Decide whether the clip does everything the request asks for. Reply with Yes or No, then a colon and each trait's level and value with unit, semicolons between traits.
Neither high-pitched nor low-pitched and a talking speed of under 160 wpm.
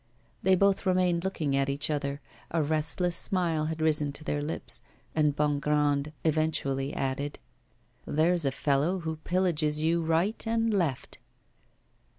Yes: medium, 155 Hz; average, 140 wpm